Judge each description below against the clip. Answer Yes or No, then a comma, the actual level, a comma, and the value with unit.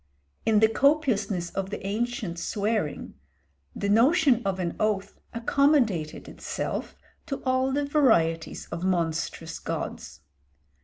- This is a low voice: No, high, 215 Hz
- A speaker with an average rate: No, slow, 115 wpm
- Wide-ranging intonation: Yes, wide, 6.6 semitones